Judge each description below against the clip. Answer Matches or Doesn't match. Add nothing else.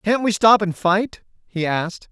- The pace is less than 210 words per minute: Matches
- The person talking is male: Matches